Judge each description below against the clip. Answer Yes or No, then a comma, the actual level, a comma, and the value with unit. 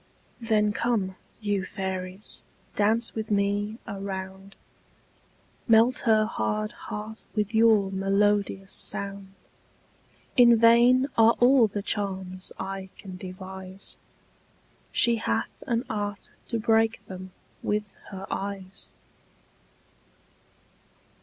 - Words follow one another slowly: Yes, slow, 100 wpm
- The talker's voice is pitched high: Yes, high, 205 Hz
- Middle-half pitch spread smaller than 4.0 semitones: Yes, narrow, 2.5 semitones